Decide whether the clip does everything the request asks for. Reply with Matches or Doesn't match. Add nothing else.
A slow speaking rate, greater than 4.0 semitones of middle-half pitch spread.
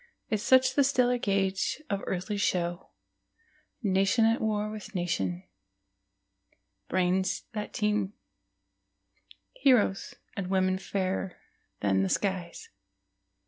Doesn't match